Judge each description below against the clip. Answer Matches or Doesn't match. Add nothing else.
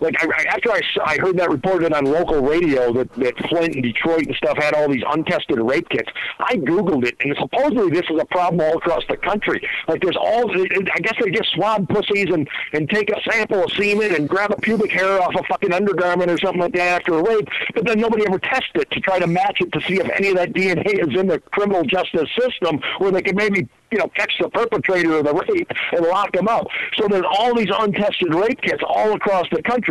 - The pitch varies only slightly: Doesn't match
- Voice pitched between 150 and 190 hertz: Matches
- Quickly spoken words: Matches